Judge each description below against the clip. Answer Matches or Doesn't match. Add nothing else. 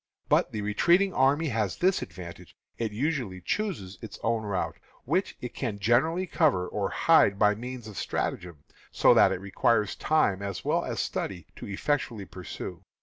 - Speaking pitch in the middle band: Doesn't match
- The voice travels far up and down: Matches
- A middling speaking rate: Matches